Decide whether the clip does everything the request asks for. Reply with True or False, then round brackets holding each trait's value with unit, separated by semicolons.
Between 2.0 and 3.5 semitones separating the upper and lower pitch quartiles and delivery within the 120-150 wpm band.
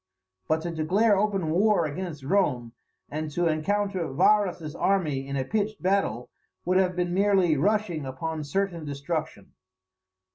False (4.6 semitones; 140 wpm)